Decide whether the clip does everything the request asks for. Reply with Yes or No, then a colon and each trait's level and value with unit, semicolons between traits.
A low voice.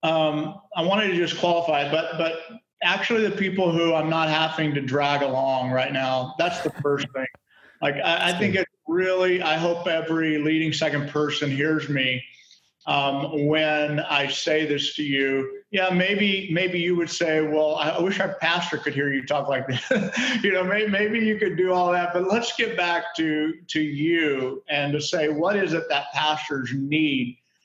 No: medium, 160 Hz